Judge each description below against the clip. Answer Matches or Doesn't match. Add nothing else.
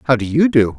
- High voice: Doesn't match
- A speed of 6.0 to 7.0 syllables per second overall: Matches